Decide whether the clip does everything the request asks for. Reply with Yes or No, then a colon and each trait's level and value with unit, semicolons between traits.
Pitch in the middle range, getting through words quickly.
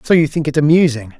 Yes: medium, 145 Hz; fast, 250 wpm